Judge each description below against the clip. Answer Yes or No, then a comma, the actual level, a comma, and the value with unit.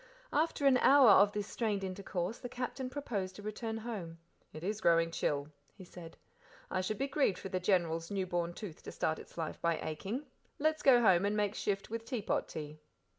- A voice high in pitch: Yes, high, 200 Hz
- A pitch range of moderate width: Yes, average, 5.0 semitones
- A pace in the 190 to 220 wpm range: Yes, average, 200 wpm